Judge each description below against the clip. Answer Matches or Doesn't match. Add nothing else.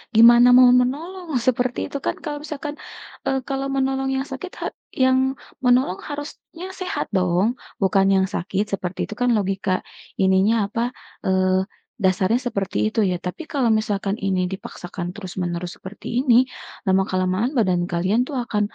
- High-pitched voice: Matches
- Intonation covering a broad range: Matches